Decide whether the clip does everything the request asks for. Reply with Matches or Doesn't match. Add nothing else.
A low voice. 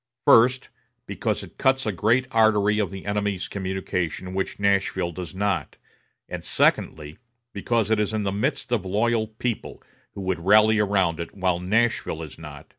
Matches